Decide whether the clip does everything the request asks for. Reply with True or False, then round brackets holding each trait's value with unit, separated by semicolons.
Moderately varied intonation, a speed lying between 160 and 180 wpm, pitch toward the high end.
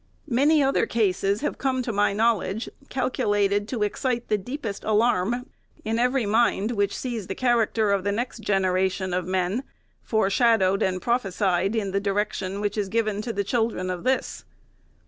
True (3.4 semitones; 165 wpm; 210 Hz)